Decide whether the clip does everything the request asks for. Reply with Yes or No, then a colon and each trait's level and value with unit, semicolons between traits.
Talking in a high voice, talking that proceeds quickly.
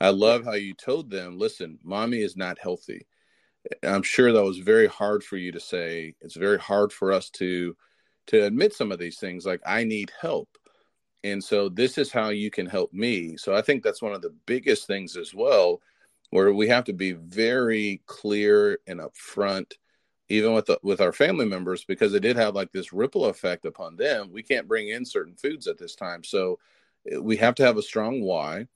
No: low, 115 Hz; fast, 210 wpm